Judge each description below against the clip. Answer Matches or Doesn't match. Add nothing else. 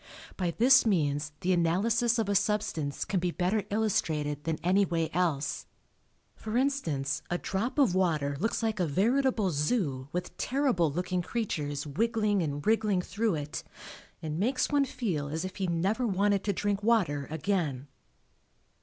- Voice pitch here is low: Doesn't match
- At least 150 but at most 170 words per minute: Matches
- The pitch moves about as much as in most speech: Doesn't match